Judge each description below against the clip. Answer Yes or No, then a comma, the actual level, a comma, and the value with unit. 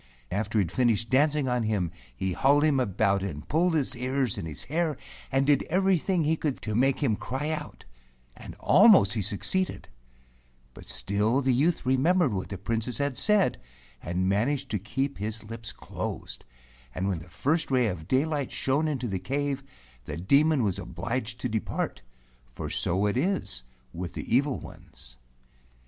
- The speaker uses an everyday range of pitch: No, wide, 6.3 semitones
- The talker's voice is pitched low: Yes, low, 125 Hz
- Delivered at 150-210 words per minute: Yes, average, 170 wpm